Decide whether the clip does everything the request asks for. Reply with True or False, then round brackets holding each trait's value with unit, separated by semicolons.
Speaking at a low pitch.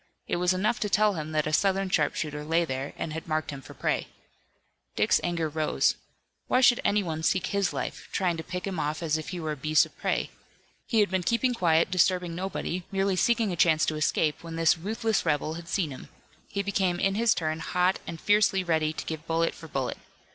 False (170 Hz)